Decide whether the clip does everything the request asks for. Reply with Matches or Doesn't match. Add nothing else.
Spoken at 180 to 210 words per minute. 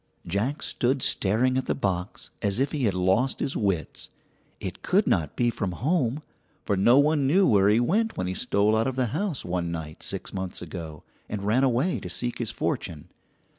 Matches